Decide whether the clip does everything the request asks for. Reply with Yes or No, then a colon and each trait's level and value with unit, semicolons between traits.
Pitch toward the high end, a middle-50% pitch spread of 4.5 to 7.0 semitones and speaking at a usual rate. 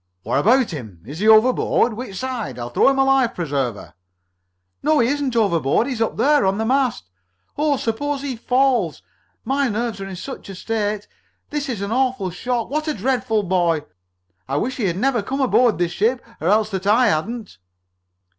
Yes: high, 225 Hz; average, 5.3 semitones; average, 190 wpm